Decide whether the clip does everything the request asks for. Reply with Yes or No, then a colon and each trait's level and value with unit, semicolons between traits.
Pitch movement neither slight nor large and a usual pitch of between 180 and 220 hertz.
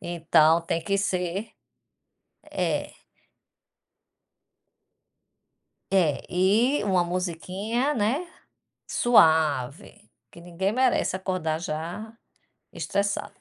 Yes: average, 3.7 semitones; medium, 185 Hz